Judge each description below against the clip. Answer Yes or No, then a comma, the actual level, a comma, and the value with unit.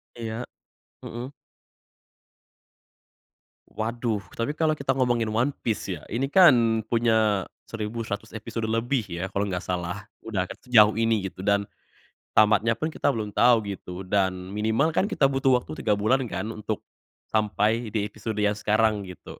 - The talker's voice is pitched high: No, low, 110 Hz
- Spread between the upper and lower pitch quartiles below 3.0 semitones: Yes, narrow, 2.6 semitones